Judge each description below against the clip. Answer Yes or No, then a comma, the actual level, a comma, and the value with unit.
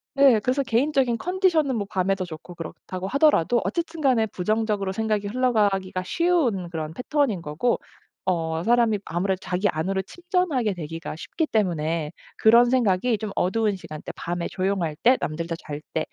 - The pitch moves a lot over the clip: Yes, wide, 6.0 semitones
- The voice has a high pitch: Yes, high, 205 Hz